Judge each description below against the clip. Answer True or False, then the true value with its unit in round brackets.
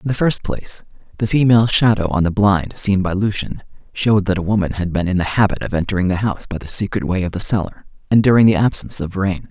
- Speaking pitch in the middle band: False (100 Hz)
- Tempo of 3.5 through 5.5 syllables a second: False (6.4 syllables/s)